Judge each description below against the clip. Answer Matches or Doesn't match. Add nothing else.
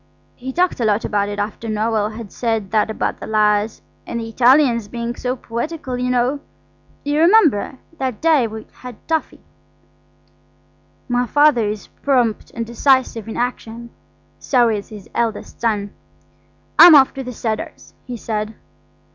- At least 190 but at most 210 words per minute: Doesn't match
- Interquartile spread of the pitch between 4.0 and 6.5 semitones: Doesn't match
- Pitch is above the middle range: Matches